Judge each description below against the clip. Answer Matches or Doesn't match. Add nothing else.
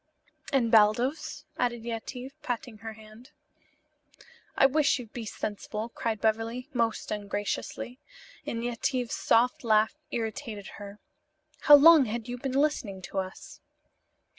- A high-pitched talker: Matches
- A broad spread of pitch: Doesn't match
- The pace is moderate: Doesn't match